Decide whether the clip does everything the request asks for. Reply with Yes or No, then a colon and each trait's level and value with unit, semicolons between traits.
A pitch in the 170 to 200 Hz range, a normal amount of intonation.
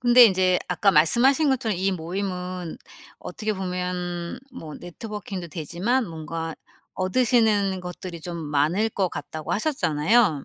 Yes: medium, 185 Hz; average, 4.2 semitones